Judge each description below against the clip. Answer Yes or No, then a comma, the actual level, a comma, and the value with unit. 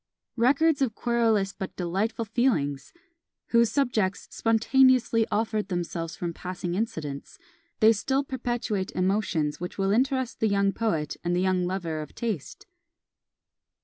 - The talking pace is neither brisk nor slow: No, slow, 130 wpm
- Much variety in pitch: No, average, 4.8 semitones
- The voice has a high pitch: Yes, high, 210 Hz